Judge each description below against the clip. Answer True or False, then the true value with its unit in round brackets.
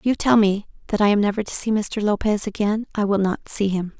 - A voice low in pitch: False (205 Hz)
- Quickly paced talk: True (270 wpm)